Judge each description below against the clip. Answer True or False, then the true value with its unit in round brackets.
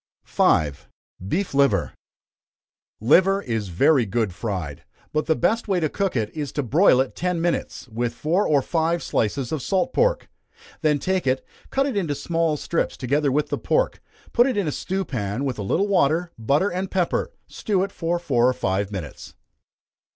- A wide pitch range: True (7.4 semitones)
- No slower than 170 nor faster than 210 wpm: True (180 wpm)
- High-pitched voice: False (150 Hz)